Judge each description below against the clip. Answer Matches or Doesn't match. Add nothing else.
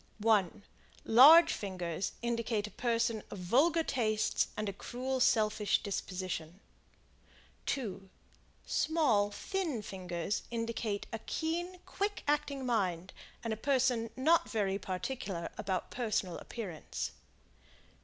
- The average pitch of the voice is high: Matches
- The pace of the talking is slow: Matches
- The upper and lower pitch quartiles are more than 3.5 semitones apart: Matches